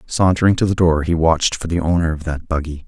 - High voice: No, very low, 85 Hz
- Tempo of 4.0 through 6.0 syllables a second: No, 6.2 syllables/s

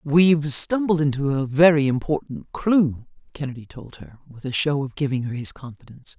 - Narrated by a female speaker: Yes, female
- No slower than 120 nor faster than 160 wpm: No, average, 175 wpm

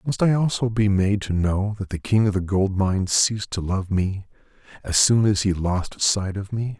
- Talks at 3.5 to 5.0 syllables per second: Yes, 4.8 syllables/s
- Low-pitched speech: Yes, low, 100 Hz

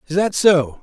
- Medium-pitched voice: Yes, medium, 175 Hz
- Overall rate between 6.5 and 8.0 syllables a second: No, 4.6 syllables/s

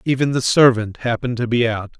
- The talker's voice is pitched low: Yes, low, 120 Hz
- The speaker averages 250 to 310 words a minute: No, fast, 210 wpm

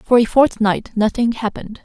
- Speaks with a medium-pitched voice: No, high, 230 Hz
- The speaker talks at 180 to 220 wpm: No, average, 165 wpm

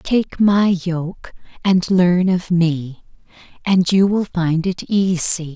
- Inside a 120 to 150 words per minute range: Yes, average, 140 wpm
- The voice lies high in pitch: No, medium, 180 Hz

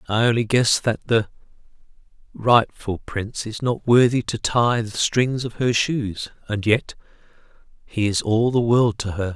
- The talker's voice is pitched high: No, low, 115 Hz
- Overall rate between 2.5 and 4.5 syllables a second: Yes, 4.2 syllables/s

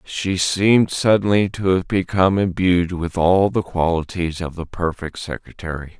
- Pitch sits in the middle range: No, very low, 90 Hz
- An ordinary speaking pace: Yes, average, 150 wpm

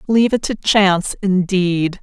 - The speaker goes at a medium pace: Yes, average, 150 wpm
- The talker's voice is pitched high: Yes, high, 195 Hz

